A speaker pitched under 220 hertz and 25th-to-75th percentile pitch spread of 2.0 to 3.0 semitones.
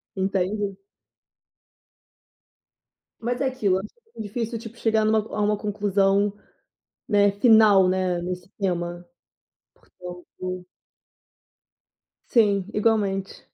Yes: high, 200 Hz; narrow, 2.6 semitones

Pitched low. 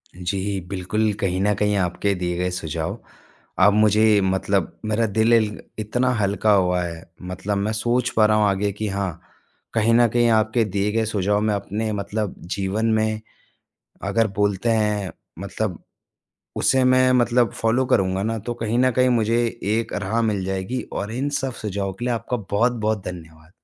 Yes: low, 105 Hz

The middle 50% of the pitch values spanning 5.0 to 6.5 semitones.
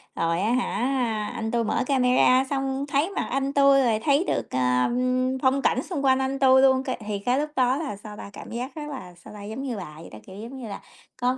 No: average, 4.2 semitones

